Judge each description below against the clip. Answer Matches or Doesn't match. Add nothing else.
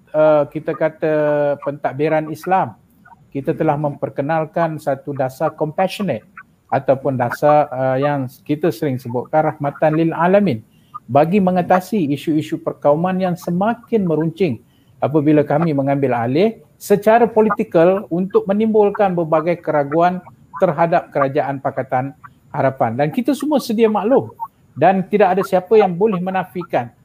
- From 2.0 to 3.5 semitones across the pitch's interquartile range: Doesn't match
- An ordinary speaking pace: Matches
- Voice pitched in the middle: Matches